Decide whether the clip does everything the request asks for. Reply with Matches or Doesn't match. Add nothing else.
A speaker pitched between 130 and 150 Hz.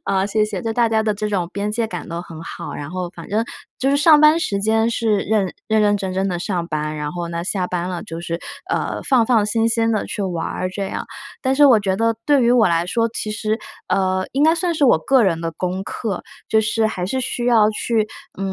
Doesn't match